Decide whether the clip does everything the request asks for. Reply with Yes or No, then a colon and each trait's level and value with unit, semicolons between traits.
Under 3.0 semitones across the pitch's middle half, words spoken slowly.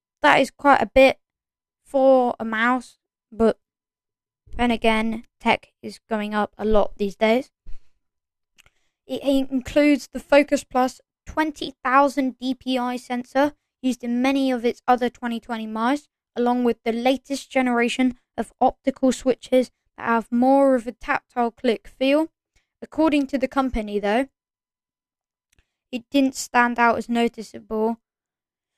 Yes: narrow, 2.5 semitones; slow, 130 wpm